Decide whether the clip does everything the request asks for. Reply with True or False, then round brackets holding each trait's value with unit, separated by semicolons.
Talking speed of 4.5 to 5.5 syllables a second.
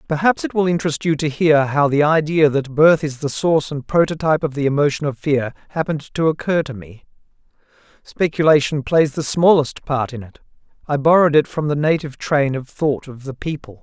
False (5.7 syllables/s)